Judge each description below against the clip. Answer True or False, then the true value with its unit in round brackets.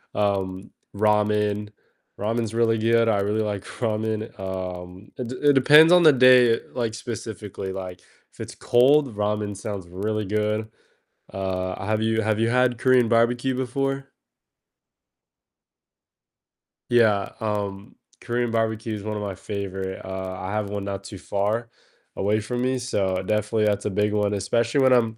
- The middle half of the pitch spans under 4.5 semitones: True (2.8 semitones)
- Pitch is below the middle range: True (105 Hz)